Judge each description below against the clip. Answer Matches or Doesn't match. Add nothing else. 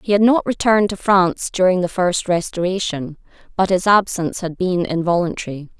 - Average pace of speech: Matches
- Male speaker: Doesn't match